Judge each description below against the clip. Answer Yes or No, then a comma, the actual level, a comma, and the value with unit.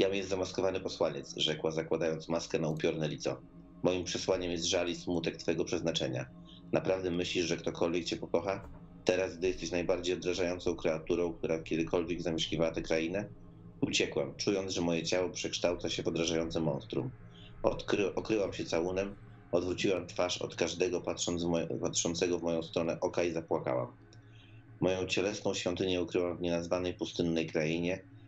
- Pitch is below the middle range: Yes, very low, 85 Hz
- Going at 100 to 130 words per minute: No, average, 155 wpm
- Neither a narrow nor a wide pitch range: No, narrow, 2.1 semitones